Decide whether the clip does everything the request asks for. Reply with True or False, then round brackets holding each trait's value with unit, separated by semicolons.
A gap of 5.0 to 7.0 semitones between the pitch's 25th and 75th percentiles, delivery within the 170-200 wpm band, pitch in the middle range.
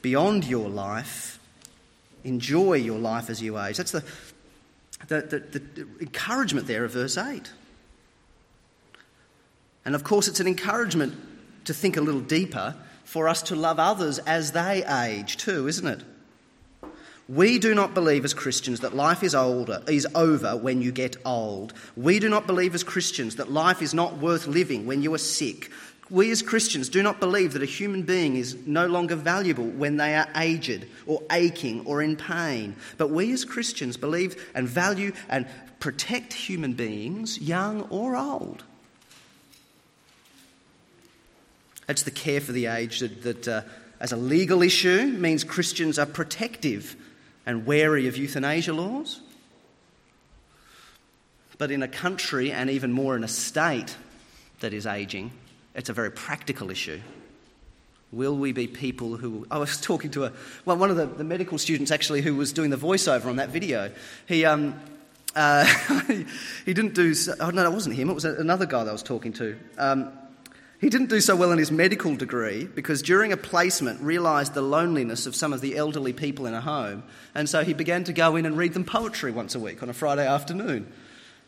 True (5.5 semitones; 180 wpm; 155 Hz)